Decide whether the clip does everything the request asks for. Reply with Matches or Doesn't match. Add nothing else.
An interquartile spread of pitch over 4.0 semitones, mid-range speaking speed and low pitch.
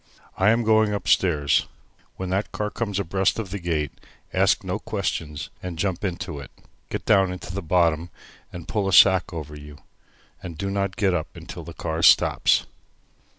Doesn't match